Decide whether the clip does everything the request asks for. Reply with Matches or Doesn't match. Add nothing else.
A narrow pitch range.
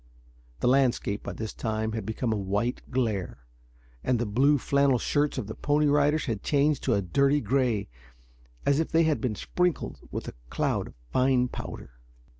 Doesn't match